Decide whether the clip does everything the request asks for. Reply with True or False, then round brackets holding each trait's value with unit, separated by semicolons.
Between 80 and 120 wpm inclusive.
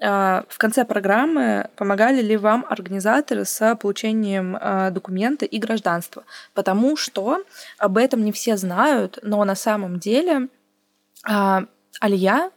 True (115 wpm)